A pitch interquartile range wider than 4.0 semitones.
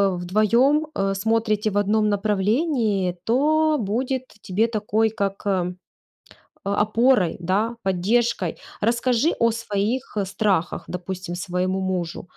No: average, 3.6 semitones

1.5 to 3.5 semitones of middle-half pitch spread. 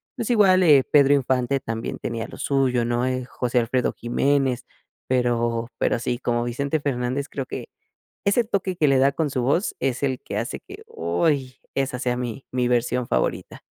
Yes: narrow, 2.5 semitones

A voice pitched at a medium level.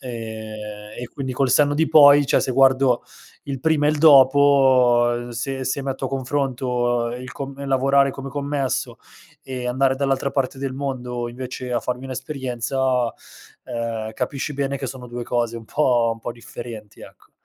No: low, 130 Hz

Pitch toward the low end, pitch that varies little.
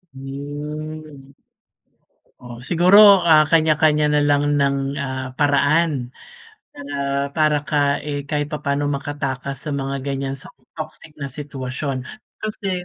No: medium, 145 Hz; narrow, 1.9 semitones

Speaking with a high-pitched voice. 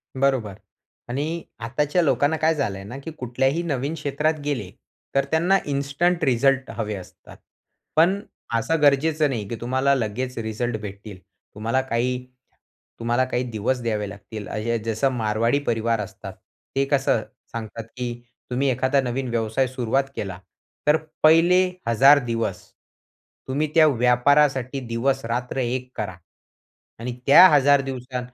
No: low, 130 Hz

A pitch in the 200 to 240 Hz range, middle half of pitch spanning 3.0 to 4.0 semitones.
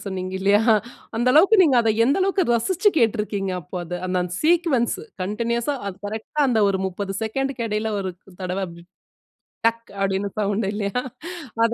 No: high, 220 Hz; average, 4.4 semitones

